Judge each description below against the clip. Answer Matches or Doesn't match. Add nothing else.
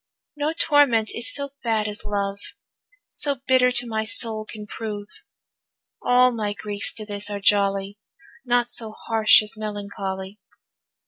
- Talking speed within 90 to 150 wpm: Matches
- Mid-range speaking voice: Doesn't match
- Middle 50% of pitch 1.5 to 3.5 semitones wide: Matches